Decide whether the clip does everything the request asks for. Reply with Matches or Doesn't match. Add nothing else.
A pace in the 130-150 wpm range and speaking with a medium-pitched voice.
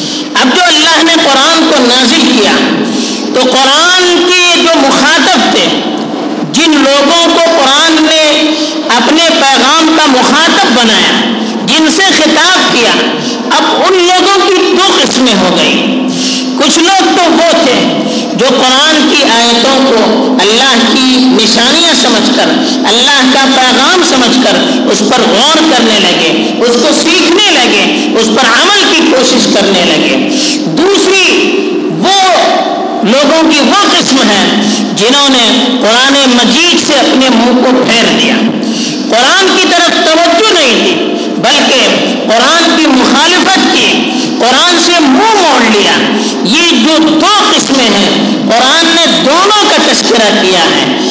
Doesn't match